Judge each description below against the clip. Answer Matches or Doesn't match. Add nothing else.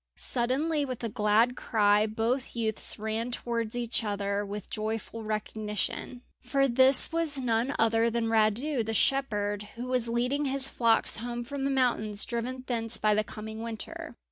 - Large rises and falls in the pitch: Doesn't match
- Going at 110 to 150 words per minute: Doesn't match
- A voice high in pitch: Matches